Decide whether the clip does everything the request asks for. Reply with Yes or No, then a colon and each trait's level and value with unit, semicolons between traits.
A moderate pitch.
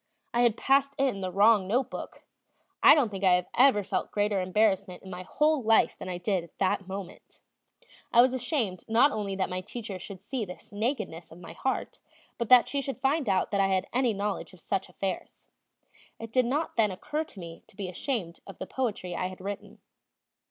No: high, 205 Hz